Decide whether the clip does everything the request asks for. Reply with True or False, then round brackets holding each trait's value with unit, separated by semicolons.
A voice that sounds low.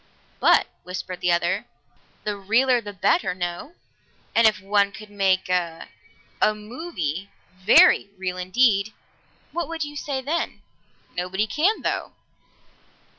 False (200 Hz)